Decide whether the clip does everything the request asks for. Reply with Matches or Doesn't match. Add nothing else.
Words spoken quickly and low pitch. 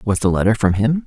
Matches